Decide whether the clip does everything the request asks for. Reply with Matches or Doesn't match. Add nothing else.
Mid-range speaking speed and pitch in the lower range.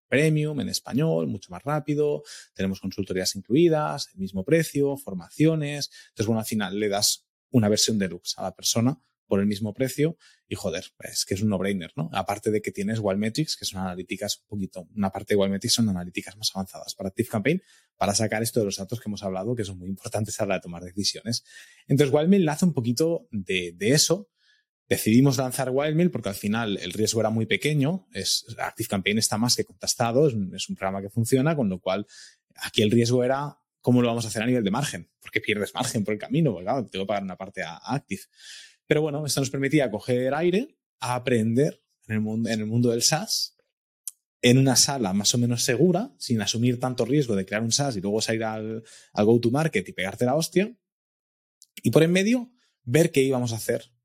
Doesn't match